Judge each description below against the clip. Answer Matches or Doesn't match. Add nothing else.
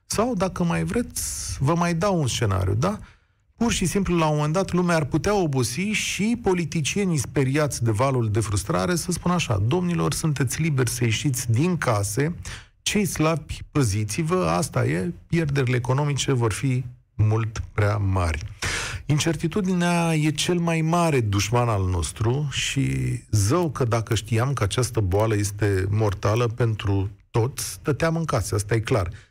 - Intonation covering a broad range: Matches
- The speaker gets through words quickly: Doesn't match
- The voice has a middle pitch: Doesn't match